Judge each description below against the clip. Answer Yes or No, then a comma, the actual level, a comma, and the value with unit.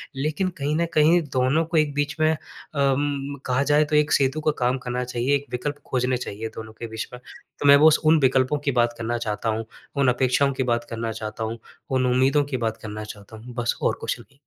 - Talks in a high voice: No, low, 130 Hz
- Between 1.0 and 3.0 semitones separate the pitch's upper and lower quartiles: No, average, 3.7 semitones